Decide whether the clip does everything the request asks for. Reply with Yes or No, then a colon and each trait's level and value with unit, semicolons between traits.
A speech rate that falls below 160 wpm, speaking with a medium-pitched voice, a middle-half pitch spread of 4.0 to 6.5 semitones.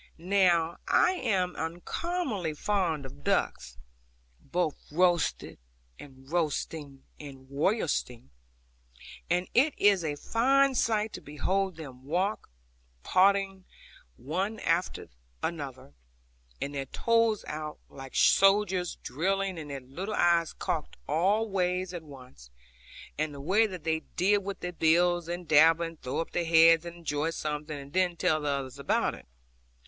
Yes: average, 140 wpm; medium, 170 Hz; average, 4.6 semitones